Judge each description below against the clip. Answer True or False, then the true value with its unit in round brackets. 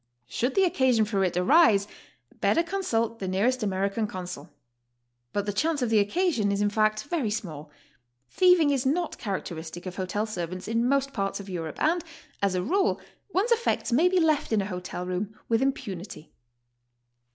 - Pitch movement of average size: False (7.0 semitones)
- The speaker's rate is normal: True (180 wpm)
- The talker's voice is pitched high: True (215 Hz)